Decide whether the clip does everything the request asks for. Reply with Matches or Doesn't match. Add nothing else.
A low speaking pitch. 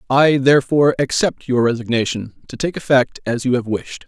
Matches